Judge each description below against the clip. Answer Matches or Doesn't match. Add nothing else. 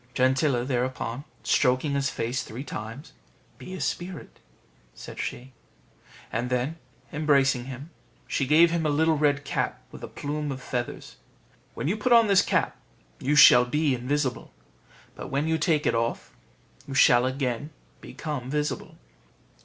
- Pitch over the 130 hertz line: Matches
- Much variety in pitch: Doesn't match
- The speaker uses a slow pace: Doesn't match